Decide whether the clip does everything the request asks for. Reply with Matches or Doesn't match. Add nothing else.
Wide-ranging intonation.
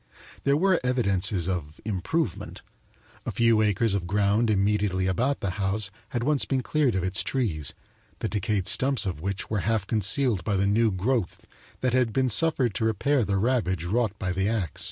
Doesn't match